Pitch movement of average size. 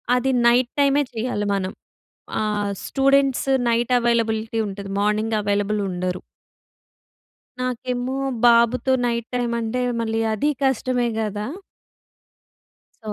Yes: average, 3.0 semitones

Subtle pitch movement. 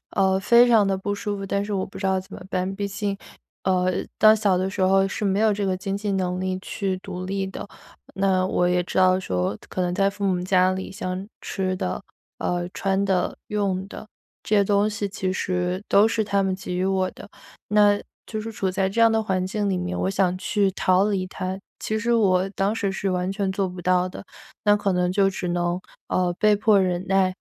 Yes: narrow, 1.6 semitones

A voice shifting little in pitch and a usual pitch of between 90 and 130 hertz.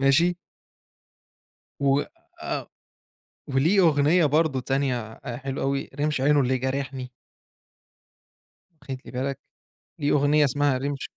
No: narrow, 1.7 semitones; medium, 140 Hz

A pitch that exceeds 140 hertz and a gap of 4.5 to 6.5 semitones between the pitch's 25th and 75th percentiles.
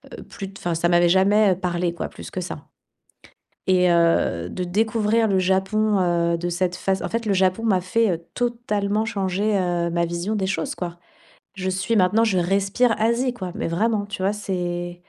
No: high, 190 Hz; average, 3.2 semitones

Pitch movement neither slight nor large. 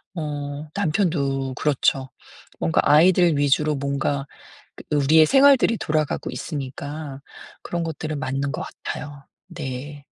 No: narrow, 2.3 semitones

